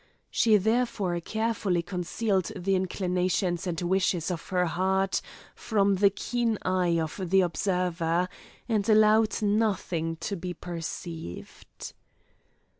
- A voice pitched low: No, medium, 185 Hz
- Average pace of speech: No, slow, 115 wpm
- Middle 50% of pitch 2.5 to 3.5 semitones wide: Yes, average, 2.9 semitones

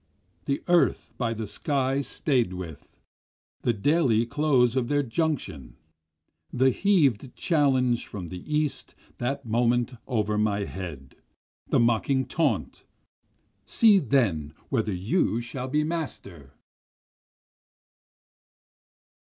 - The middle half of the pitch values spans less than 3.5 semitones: No, average, 5.1 semitones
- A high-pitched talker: No, low, 125 Hz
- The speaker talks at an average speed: No, slow, 105 wpm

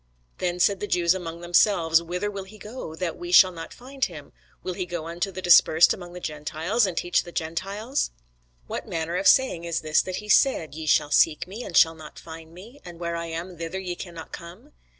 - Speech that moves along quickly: Yes, fast, 220 wpm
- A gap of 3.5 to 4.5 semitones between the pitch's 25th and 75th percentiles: No, average, 2.7 semitones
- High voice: No, medium, 175 Hz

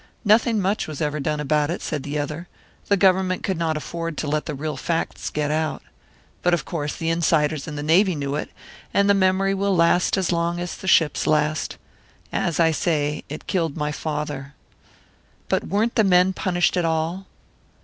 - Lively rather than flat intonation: No, average, 3.5 semitones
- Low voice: No, medium, 165 Hz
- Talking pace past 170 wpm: Yes, average, 190 wpm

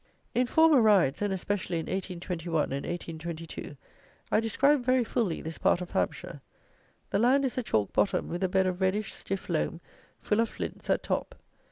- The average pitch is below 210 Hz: Yes, high, 190 Hz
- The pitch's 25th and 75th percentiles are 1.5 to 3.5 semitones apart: No, average, 5.0 semitones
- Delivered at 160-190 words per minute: Yes, average, 180 wpm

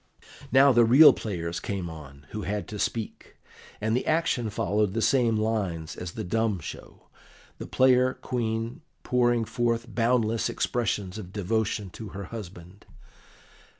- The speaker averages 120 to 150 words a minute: Yes, average, 145 wpm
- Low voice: Yes, low, 110 Hz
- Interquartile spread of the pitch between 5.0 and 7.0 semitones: No, average, 3.5 semitones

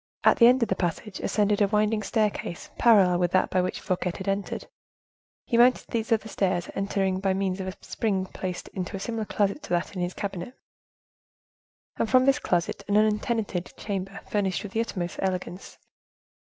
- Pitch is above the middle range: Yes, high, 195 Hz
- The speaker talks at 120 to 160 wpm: No, average, 185 wpm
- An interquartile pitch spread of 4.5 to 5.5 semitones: No, average, 2.7 semitones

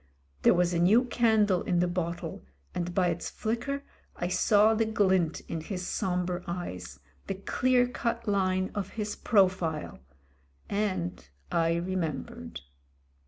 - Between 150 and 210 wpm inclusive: No, slow, 135 wpm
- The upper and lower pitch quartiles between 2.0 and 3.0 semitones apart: No, average, 3.5 semitones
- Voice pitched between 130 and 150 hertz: No, medium, 185 Hz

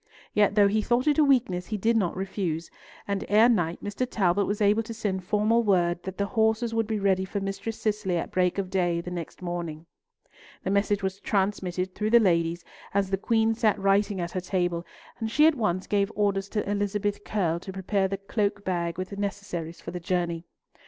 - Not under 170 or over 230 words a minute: Yes, fast, 205 wpm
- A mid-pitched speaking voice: No, high, 200 Hz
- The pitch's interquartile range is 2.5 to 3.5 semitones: Yes, average, 2.8 semitones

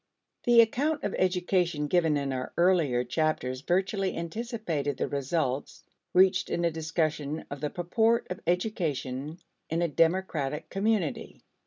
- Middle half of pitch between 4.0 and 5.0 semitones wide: Yes, average, 4.3 semitones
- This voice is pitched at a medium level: Yes, medium, 170 Hz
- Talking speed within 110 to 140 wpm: Yes, slow, 135 wpm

